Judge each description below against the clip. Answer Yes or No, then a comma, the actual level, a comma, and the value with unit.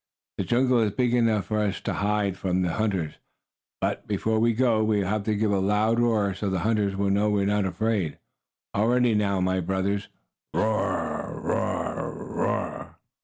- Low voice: Yes, low, 105 Hz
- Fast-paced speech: No, average, 175 wpm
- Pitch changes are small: Yes, narrow, 2.1 semitones